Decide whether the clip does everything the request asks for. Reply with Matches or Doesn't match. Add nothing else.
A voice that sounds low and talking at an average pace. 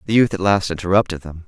Doesn't match